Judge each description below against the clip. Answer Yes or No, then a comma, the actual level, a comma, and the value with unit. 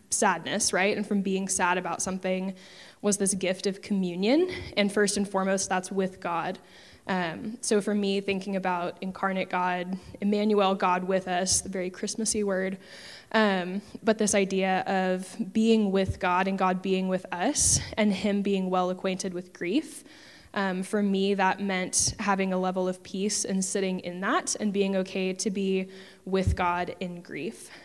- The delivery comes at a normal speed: Yes, average, 170 wpm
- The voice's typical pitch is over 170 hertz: Yes, high, 190 Hz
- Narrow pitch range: Yes, narrow, 1.7 semitones